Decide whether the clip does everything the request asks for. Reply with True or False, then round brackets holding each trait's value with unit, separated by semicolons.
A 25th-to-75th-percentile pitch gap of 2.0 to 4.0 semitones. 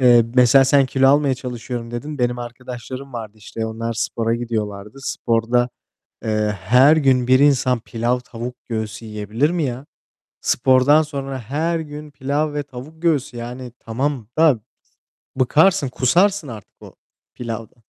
True (3.4 semitones)